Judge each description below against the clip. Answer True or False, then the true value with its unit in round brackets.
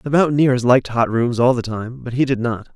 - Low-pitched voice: True (125 Hz)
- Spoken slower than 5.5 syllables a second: False (5.7 syllables/s)